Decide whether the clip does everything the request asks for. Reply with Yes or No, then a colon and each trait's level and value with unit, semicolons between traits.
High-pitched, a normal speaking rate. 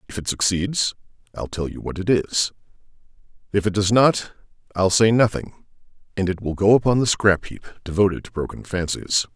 No: low, 100 Hz; average, 180 wpm